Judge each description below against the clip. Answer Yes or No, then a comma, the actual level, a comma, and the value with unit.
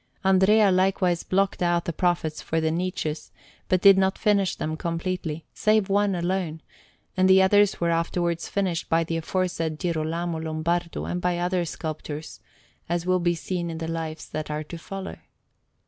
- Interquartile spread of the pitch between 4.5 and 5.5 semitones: No, narrow, 2.5 semitones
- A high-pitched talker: No, medium, 175 Hz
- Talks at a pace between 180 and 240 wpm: No, average, 165 wpm